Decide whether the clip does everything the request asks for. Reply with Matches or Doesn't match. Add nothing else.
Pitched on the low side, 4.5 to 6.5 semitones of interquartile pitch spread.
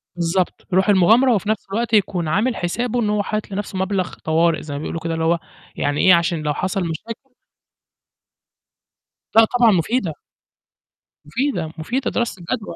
Doesn't match